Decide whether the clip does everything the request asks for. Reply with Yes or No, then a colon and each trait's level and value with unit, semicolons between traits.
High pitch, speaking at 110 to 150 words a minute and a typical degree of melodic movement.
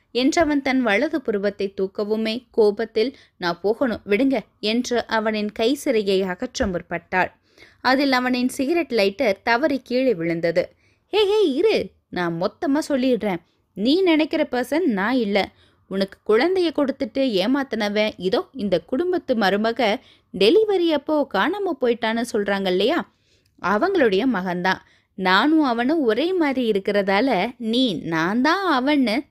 No: high, 245 Hz; average, 120 wpm; wide, 6.4 semitones